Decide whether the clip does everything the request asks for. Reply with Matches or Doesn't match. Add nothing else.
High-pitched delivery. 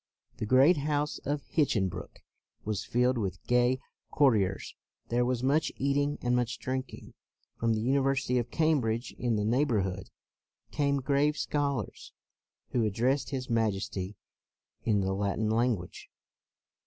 Doesn't match